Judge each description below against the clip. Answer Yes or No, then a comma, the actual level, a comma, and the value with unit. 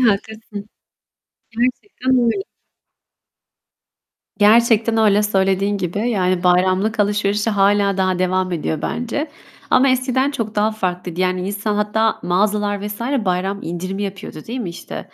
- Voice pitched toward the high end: Yes, high, 205 Hz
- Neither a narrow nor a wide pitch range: Yes, average, 3.0 semitones